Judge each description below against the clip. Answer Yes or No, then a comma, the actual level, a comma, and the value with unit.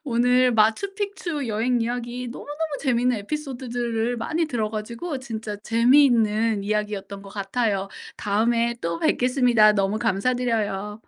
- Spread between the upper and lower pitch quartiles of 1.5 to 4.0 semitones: Yes, average, 3.0 semitones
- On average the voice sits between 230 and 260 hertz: Yes, high, 235 Hz